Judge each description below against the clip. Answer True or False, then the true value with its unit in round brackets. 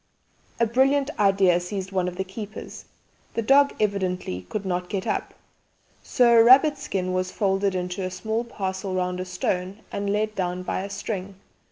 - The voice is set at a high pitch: True (195 Hz)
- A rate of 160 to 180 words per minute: True (175 wpm)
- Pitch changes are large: False (2.9 semitones)